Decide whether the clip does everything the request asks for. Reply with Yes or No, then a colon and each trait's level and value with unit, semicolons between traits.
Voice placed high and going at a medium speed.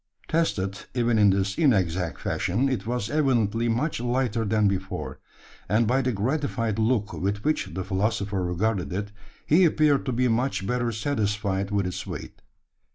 No: low, 110 Hz; average, 160 wpm